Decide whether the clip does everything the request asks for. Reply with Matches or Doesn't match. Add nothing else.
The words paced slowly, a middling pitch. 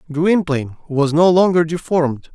Matches